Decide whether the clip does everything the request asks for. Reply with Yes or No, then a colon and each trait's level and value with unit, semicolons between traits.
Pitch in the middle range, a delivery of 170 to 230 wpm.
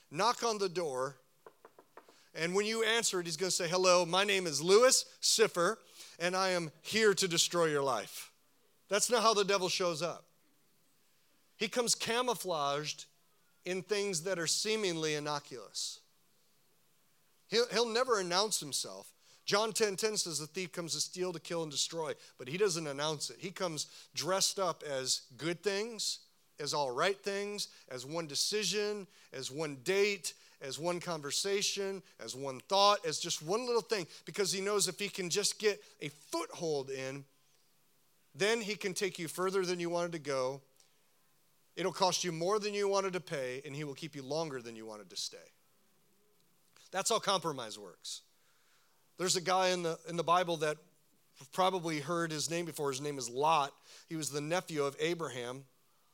Yes: medium, 180 Hz; average, 175 wpm